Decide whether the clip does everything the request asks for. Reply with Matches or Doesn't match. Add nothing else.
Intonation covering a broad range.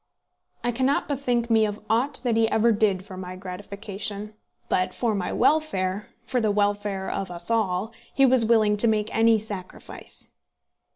Doesn't match